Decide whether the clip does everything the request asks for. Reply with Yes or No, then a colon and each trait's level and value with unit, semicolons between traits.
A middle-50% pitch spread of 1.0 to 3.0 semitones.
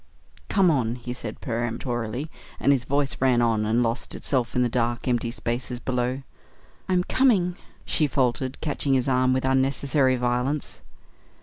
Yes: narrow, 2.4 semitones